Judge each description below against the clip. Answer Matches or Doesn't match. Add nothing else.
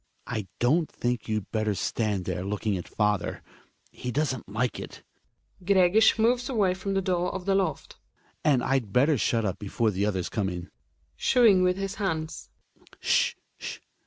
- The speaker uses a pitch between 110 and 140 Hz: Matches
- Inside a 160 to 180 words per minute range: Matches